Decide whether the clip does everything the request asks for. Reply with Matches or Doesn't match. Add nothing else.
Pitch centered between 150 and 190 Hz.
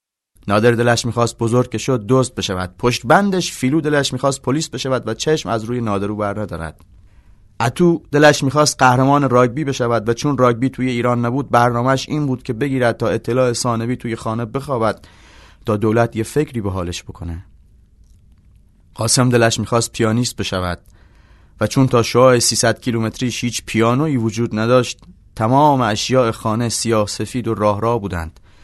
Doesn't match